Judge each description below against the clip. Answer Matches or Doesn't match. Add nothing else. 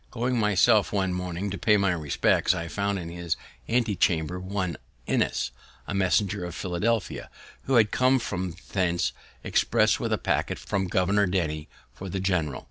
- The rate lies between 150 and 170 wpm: Matches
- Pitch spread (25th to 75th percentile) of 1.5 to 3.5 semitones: Matches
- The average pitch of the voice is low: Matches